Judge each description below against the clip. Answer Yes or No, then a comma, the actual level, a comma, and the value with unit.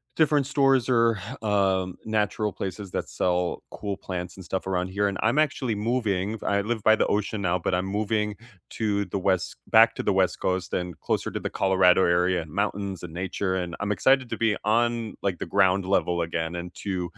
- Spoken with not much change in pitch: No, average, 3.0 semitones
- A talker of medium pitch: No, low, 100 Hz